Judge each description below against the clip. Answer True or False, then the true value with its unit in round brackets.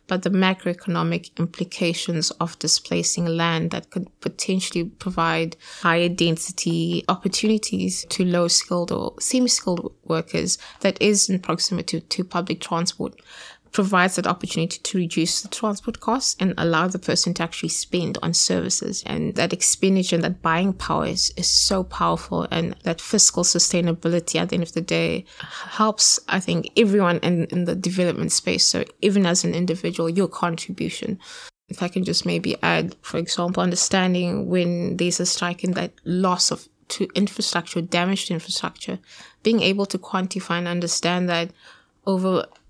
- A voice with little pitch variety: True (2.1 semitones)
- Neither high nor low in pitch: True (175 Hz)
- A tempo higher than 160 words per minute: False (155 wpm)